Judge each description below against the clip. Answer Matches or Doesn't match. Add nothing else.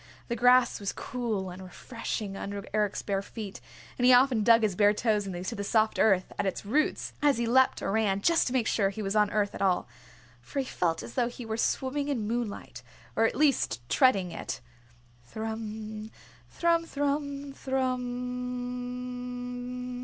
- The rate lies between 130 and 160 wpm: Doesn't match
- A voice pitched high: Matches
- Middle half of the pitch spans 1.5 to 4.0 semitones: Matches